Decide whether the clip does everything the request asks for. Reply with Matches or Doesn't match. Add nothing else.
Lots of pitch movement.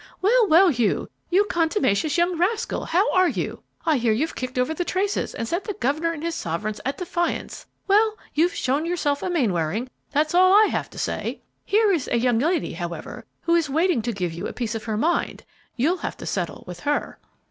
Matches